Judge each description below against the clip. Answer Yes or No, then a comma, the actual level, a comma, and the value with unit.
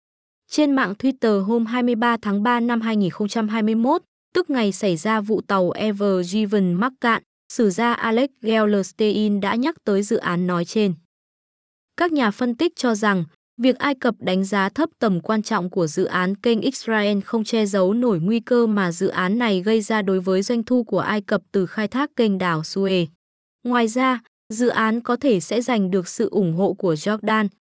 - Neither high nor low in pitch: No, high, 215 Hz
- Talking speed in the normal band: Yes, average, 195 wpm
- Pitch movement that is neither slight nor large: Yes, average, 3.5 semitones